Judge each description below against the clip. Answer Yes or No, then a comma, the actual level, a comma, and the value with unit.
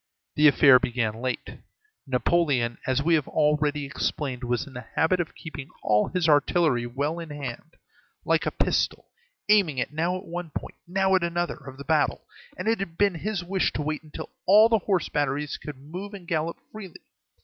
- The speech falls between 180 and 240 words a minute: Yes, average, 185 wpm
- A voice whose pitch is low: No, medium, 155 Hz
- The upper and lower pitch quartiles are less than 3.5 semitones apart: No, average, 4.4 semitones